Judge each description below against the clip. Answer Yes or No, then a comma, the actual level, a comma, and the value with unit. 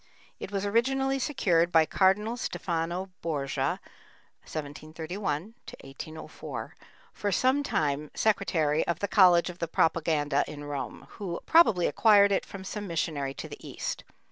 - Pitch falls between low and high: Yes, medium, 175 Hz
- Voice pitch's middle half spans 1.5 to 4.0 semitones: No, average, 4.8 semitones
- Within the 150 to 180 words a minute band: No, slow, 135 wpm